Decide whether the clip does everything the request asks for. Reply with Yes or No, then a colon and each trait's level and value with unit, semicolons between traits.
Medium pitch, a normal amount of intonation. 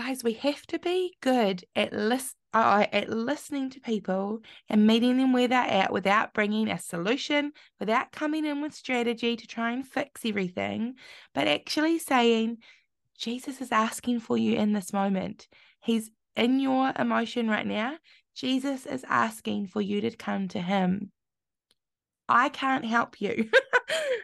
No: high, 235 Hz; average, 3.7 semitones